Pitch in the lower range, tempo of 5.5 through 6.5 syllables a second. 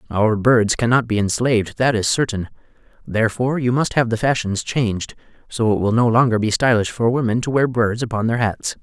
Yes: low, 115 Hz; 5.6 syllables/s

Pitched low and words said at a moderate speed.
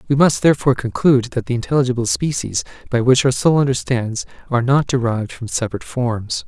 Yes: low, 125 Hz; average, 175 wpm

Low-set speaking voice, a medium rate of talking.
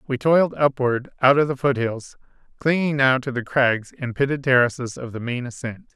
Yes: low, 130 Hz; average, 190 wpm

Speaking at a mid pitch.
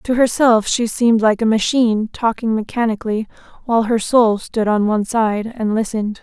No: high, 225 Hz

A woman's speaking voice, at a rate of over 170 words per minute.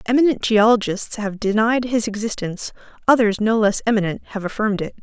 No: female; average, 155 wpm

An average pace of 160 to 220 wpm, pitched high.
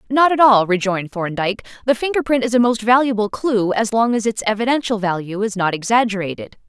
Yes: average, 200 wpm; high, 220 Hz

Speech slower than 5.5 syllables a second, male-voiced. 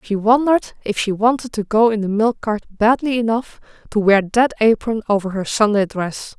No: 5.0 syllables/s; female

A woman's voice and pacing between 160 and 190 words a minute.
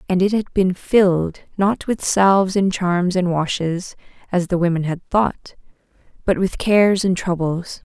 Yes: female; average, 165 wpm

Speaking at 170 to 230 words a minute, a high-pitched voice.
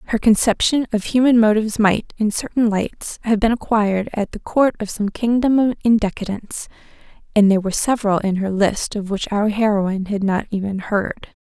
Yes: average, 185 wpm; high, 210 Hz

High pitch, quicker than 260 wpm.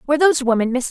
No: very high, 270 Hz; average, 200 wpm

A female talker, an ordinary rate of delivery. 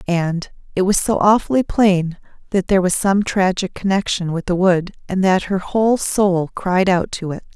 Yes: female; average, 190 wpm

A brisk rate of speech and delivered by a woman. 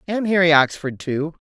No: average, 165 wpm; female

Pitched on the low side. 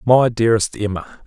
Yes: low, 110 Hz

